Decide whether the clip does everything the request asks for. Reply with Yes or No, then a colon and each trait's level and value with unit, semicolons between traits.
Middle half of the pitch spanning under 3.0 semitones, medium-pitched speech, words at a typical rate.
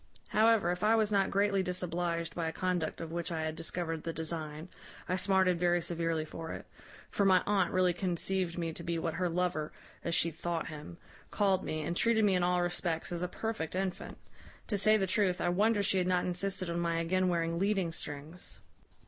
No: narrow, 2.4 semitones; medium, 175 Hz; fast, 210 wpm